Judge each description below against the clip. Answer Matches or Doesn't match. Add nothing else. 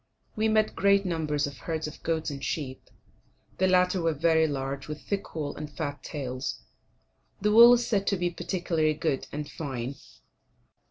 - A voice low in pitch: Doesn't match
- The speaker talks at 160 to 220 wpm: Matches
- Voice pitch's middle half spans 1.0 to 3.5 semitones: Doesn't match